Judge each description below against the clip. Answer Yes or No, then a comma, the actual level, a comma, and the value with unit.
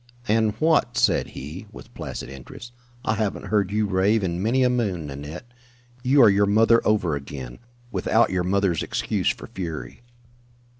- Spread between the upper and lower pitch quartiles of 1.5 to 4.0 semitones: No, average, 4.7 semitones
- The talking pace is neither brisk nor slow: Yes, average, 160 wpm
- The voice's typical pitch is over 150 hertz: No, low, 100 Hz